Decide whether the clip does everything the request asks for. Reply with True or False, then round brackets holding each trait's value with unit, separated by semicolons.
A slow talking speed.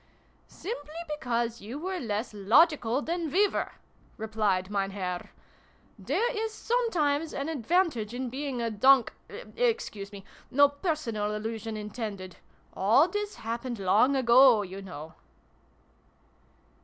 True (125 wpm)